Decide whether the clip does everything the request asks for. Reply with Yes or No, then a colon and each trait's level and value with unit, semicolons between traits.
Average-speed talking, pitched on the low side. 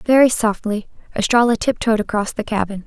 No: average, 145 wpm; high, 220 Hz